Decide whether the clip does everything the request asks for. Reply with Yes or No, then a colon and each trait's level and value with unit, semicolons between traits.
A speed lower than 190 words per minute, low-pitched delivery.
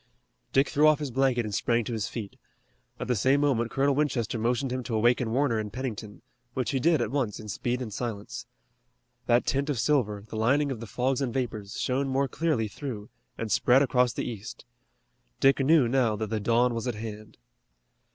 No: average, 200 wpm; low, 125 Hz